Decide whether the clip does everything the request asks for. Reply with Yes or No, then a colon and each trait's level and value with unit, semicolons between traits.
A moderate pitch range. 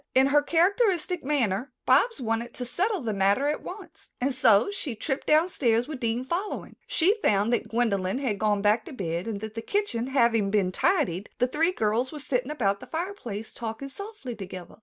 No: wide, 6.4 semitones